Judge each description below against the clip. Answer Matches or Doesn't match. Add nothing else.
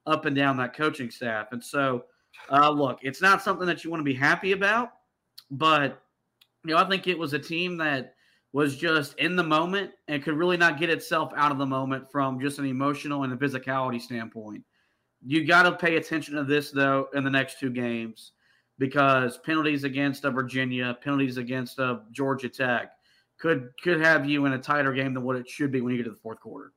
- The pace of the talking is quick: Matches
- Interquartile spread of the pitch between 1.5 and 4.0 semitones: Matches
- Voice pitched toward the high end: Doesn't match